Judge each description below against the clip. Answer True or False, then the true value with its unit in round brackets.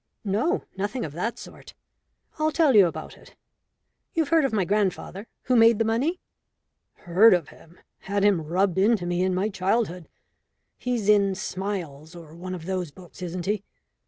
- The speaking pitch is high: True (195 Hz)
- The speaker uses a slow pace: False (170 wpm)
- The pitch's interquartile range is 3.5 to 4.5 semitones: True (4.1 semitones)